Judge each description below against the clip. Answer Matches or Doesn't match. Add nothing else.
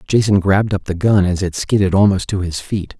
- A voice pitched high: Doesn't match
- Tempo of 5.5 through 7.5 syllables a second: Matches